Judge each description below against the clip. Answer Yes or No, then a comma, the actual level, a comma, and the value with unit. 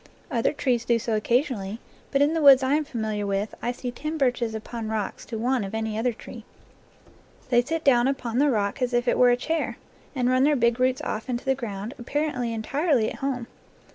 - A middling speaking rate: No, fast, 215 wpm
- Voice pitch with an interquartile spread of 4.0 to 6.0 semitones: No, average, 3.4 semitones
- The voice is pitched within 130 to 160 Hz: No, high, 245 Hz